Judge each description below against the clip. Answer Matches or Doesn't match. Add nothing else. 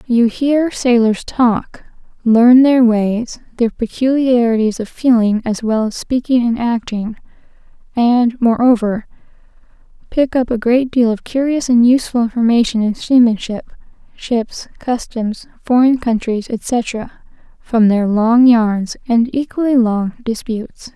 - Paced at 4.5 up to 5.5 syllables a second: Doesn't match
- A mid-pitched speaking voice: Doesn't match